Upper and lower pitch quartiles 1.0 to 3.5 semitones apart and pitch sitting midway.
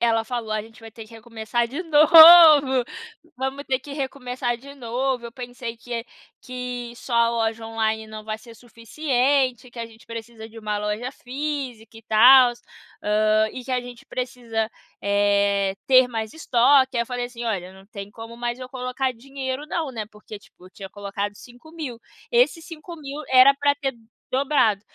No: average, 3.1 semitones; high, 240 Hz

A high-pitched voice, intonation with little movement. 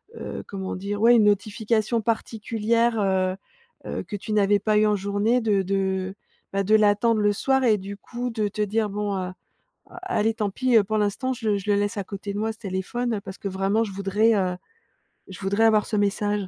Yes: high, 210 Hz; narrow, 2.1 semitones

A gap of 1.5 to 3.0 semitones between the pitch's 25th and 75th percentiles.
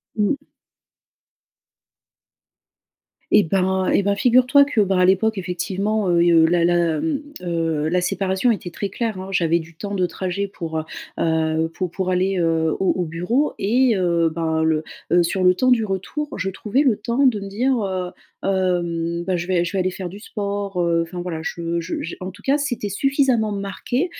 No: average, 3.4 semitones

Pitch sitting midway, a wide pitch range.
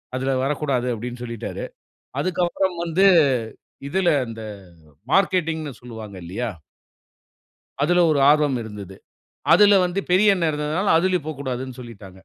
Yes: medium, 150 Hz; wide, 6.5 semitones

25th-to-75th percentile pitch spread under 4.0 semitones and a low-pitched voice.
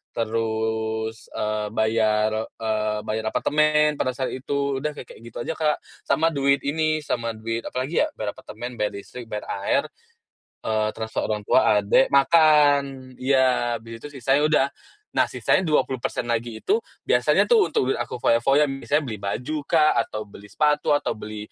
No: average, 4.8 semitones; low, 125 Hz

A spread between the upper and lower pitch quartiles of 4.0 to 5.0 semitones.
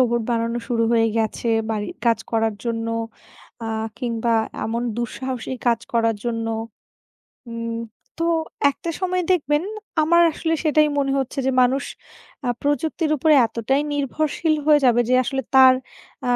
Yes: average, 4.3 semitones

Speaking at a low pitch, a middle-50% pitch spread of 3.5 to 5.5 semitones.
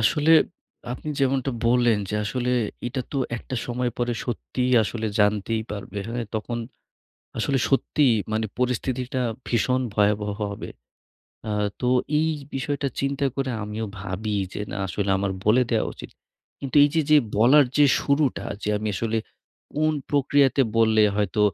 Yes: low, 120 Hz; average, 4.0 semitones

